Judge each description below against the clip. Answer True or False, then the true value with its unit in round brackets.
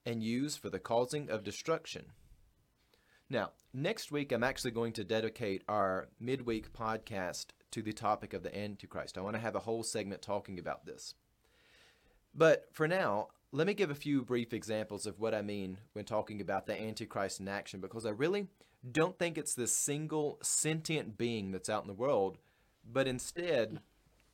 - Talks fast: False (180 wpm)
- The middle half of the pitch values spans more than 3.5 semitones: True (4.7 semitones)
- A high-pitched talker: False (110 Hz)